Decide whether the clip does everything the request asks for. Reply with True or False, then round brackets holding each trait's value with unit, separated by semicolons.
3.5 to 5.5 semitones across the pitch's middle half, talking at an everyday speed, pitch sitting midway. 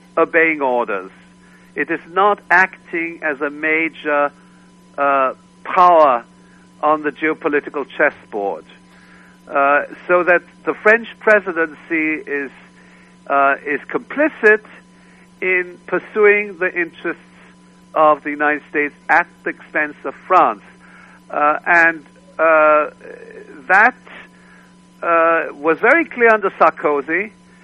False (4.0 semitones; 105 wpm; 165 Hz)